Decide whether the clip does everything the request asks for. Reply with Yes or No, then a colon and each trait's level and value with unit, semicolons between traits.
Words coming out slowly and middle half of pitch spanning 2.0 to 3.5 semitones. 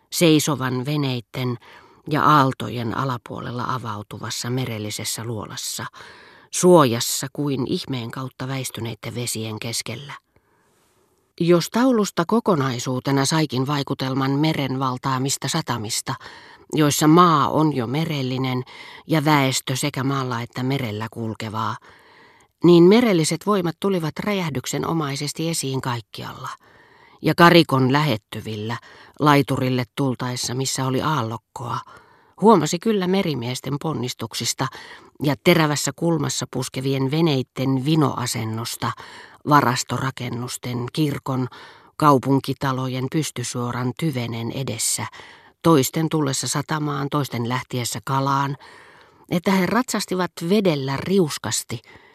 No: slow, 90 wpm; average, 4.1 semitones